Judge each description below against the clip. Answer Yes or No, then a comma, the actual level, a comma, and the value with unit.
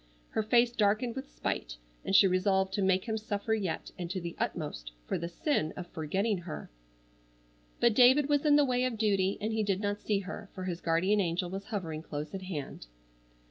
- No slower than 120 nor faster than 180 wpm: No, fast, 205 wpm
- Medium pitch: No, high, 195 Hz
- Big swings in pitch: No, average, 3.9 semitones